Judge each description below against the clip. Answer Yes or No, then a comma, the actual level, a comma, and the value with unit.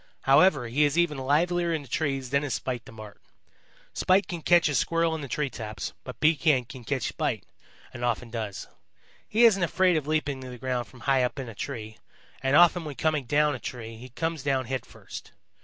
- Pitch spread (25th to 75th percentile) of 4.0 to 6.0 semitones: Yes, average, 4.3 semitones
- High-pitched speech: No, medium, 140 Hz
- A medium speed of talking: No, fast, 210 wpm